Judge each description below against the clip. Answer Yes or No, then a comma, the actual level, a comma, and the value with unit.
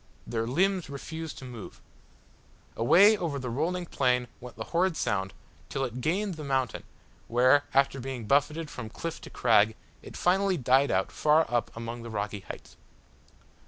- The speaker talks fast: No, average, 160 wpm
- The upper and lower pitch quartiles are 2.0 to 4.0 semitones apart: No, wide, 5.6 semitones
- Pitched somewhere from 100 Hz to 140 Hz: Yes, low, 135 Hz